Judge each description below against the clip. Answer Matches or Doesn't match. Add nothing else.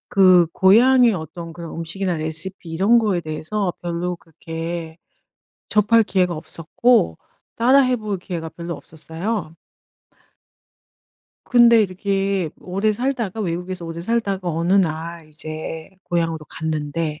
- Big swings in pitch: Doesn't match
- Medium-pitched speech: Matches